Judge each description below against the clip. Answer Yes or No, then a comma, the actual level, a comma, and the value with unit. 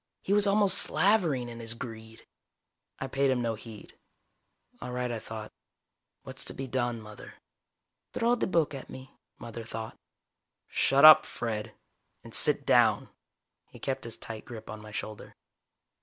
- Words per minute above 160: No, average, 155 wpm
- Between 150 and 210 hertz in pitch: No, low, 120 Hz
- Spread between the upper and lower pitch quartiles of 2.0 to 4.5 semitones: Yes, average, 3.6 semitones